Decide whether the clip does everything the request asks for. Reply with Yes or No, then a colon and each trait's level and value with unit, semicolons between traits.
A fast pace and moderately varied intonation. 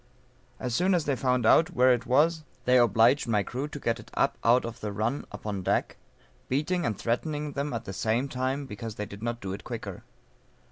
Yes: fast, 215 wpm; average, 4.1 semitones